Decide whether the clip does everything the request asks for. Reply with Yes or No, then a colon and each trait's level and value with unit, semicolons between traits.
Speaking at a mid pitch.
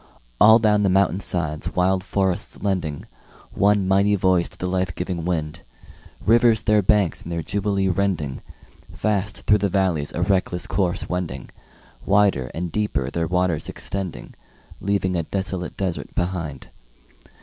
No: very low, 95 Hz